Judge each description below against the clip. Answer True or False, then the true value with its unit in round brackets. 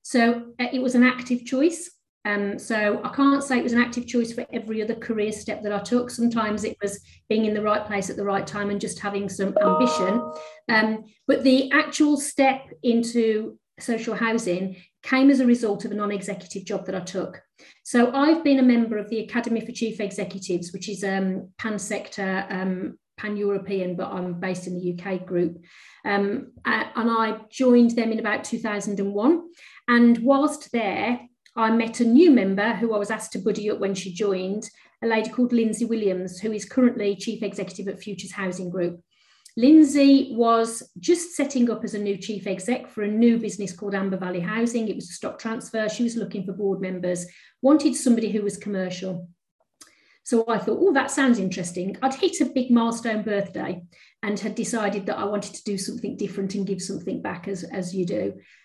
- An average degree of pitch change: True (3.5 semitones)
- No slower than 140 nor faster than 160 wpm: False (195 wpm)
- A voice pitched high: True (215 Hz)